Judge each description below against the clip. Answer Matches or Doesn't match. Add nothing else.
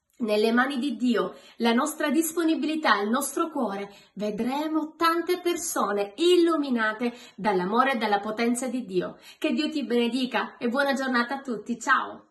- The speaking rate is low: Doesn't match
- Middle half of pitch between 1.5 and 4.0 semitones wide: Doesn't match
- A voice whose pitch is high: Matches